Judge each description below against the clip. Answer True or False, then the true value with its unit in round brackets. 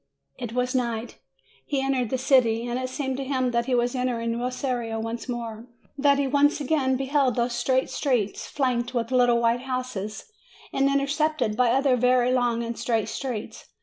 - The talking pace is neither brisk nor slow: True (175 wpm)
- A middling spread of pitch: False (2.1 semitones)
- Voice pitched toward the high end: True (250 Hz)